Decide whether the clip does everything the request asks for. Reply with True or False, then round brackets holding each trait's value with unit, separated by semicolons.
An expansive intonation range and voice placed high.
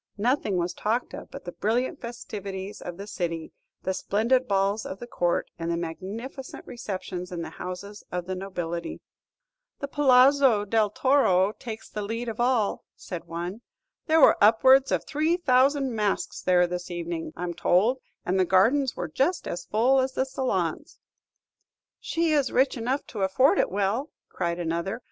True (6.2 semitones; 210 Hz)